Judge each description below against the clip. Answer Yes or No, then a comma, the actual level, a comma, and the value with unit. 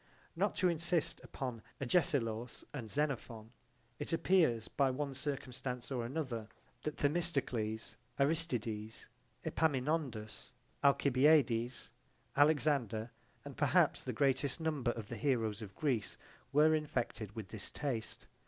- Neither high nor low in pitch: No, low, 130 Hz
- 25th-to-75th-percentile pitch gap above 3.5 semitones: Yes, average, 4.6 semitones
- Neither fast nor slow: No, slow, 115 wpm